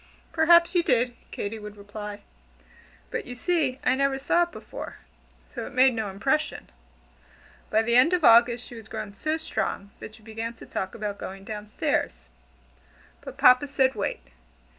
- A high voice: Yes, high, 235 Hz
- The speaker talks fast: No, average, 170 wpm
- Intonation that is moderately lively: Yes, average, 4.7 semitones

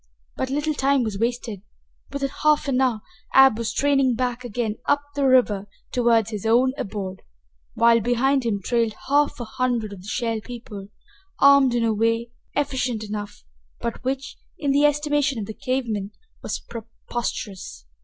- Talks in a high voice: Yes, high, 240 Hz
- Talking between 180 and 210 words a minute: No, average, 165 wpm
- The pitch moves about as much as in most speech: Yes, average, 3.6 semitones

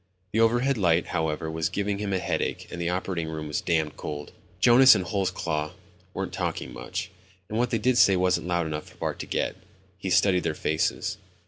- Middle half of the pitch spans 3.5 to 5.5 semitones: Yes, average, 4.2 semitones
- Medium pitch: No, very low, 90 Hz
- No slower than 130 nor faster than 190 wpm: No, average, 200 wpm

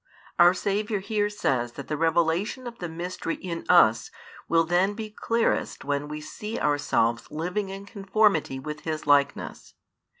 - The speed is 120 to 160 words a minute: Yes, average, 155 wpm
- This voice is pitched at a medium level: Yes, medium, 175 Hz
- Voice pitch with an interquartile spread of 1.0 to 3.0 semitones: No, average, 5.2 semitones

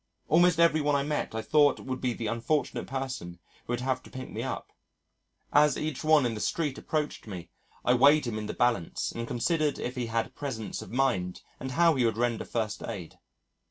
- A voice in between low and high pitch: No, low, 130 Hz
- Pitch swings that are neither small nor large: Yes, average, 4.3 semitones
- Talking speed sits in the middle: No, fast, 210 wpm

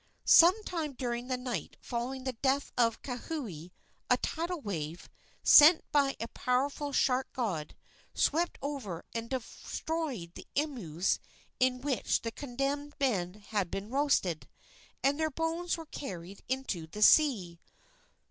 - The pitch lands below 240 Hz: No, very high, 255 Hz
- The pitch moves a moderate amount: No, wide, 5.8 semitones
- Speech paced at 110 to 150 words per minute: Yes, slow, 135 wpm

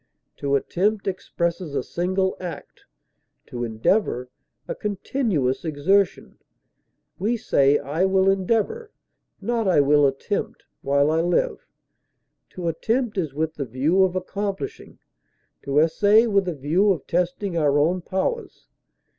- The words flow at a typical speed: No, slow, 130 wpm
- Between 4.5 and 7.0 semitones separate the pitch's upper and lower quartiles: Yes, wide, 5.4 semitones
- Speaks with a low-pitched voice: No, medium, 180 Hz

